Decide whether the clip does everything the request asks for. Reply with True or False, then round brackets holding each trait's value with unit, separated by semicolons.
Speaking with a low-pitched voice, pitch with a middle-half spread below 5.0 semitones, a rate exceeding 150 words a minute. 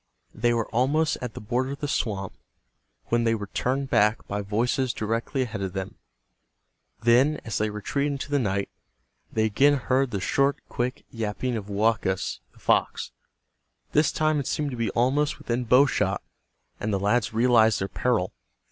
True (120 Hz; 4.0 semitones; 175 wpm)